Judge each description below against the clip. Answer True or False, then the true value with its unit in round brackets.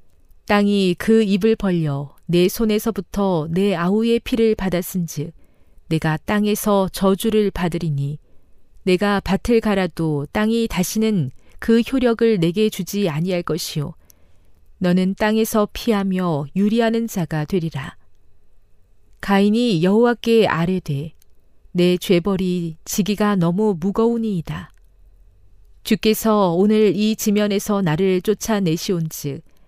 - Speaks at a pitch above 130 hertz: True (185 Hz)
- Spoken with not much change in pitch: False (5.4 semitones)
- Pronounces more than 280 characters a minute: False (245 characters per minute)